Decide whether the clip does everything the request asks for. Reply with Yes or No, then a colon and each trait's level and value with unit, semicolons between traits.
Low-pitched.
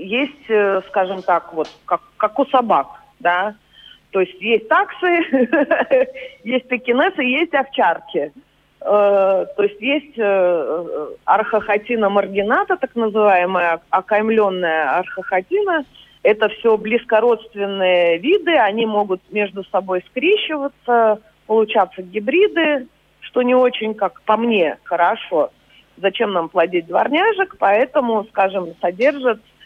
No: high, 220 Hz